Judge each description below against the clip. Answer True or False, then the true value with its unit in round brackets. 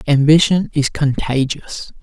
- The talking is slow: True (90 wpm)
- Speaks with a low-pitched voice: False (145 Hz)